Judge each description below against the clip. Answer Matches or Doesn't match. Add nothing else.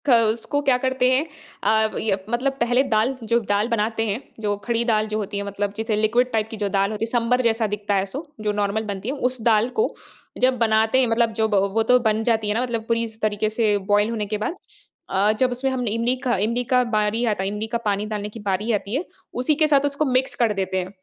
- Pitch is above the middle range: Matches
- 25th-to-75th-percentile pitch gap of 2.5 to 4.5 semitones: Matches